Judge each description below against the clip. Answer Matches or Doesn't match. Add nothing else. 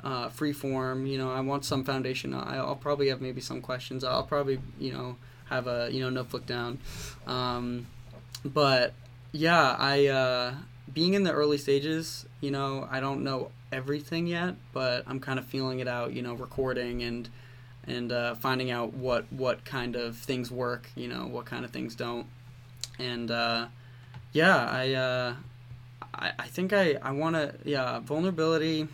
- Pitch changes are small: Matches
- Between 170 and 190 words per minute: Matches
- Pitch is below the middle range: Matches